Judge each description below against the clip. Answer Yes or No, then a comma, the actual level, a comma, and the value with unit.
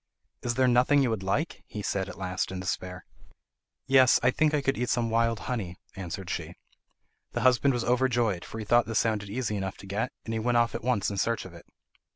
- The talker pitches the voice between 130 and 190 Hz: No, low, 115 Hz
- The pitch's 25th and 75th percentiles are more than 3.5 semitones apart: Yes, average, 4.1 semitones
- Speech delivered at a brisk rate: Yes, fast, 225 wpm